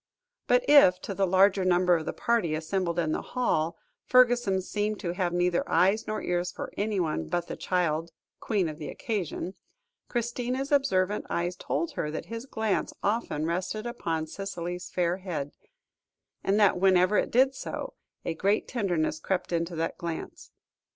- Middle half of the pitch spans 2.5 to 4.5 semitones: Yes, average, 3.9 semitones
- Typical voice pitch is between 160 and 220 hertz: Yes, medium, 185 Hz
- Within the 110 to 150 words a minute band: No, average, 165 wpm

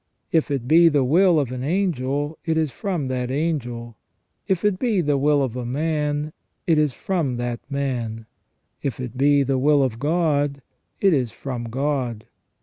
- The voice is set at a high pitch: No, medium, 140 Hz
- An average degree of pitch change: Yes, average, 3.9 semitones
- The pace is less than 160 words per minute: No, average, 170 wpm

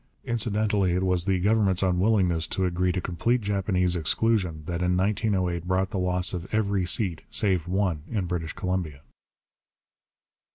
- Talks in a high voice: No, very low, 90 Hz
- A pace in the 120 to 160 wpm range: Yes, average, 150 wpm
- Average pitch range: No, narrow, 2.3 semitones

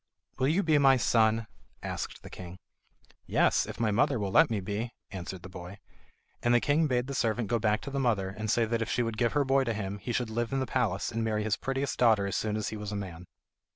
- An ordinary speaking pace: No, fast, 255 wpm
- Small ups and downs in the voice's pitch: No, average, 3.7 semitones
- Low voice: Yes, low, 115 Hz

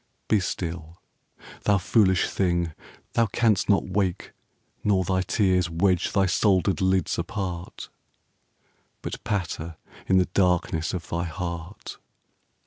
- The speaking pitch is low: Yes, very low, 95 Hz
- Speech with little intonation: Yes, narrow, 2.2 semitones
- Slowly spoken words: Yes, slow, 120 wpm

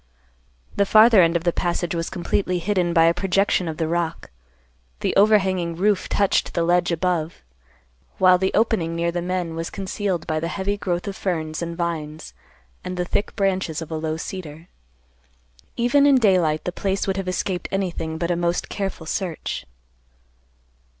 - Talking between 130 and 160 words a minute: No, average, 170 wpm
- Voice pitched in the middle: Yes, medium, 175 Hz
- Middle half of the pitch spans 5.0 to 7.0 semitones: No, narrow, 2.6 semitones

